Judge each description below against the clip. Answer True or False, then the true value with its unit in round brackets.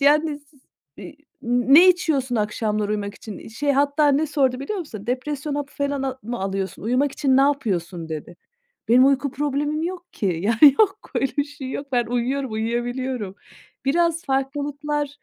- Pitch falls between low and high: False (270 Hz)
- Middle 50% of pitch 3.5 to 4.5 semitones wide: True (3.9 semitones)